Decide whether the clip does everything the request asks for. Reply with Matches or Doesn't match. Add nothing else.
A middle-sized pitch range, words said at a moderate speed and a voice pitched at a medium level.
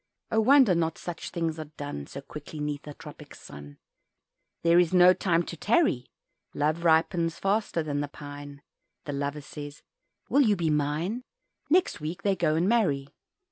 Matches